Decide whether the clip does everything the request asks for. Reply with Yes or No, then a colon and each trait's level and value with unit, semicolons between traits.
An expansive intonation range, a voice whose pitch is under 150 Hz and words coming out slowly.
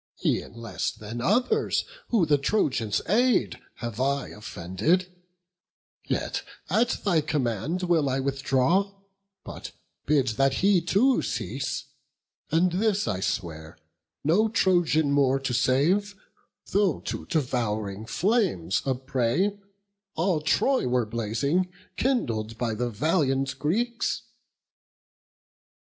Yes: wide, 8.1 semitones; medium, 140 Hz; slow, 110 wpm